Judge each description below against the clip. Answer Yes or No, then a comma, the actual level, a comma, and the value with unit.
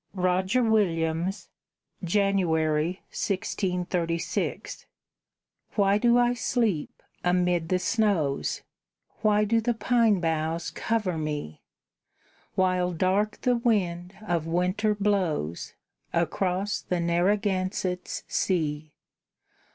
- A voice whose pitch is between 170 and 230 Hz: Yes, medium, 185 Hz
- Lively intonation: No, average, 3.7 semitones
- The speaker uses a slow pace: Yes, slow, 90 wpm